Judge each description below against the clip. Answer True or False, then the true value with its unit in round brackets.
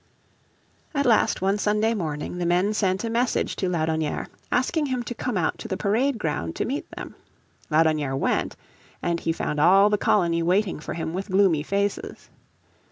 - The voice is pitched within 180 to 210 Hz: True (190 Hz)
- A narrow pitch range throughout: False (4.8 semitones)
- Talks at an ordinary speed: True (175 wpm)